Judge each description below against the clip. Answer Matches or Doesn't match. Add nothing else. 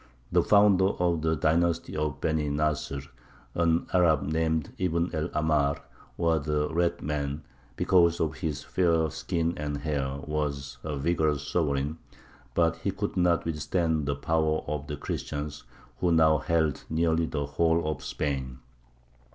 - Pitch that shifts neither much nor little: Doesn't match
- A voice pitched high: Doesn't match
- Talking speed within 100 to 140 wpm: Doesn't match